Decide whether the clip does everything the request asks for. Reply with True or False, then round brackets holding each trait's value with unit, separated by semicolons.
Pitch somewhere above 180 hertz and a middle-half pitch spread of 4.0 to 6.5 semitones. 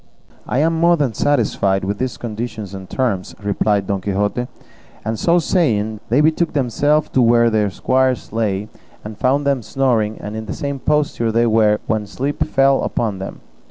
False (115 Hz; 4.7 semitones)